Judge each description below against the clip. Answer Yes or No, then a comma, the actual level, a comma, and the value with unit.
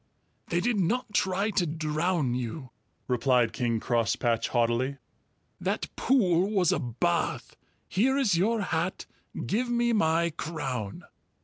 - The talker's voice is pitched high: No, medium, 165 Hz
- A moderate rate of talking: No, slow, 125 wpm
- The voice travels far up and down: Yes, wide, 8.5 semitones